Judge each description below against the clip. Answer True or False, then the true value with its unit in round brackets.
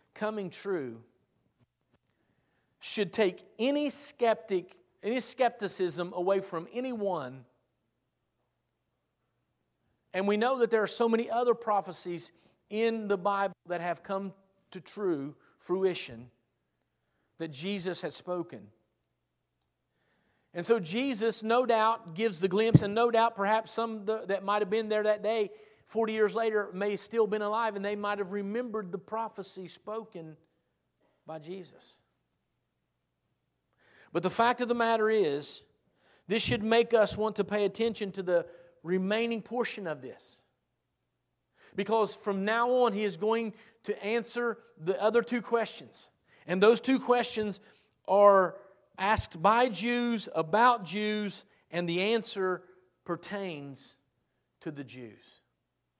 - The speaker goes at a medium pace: False (130 wpm)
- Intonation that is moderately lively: True (4.3 semitones)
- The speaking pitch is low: False (205 Hz)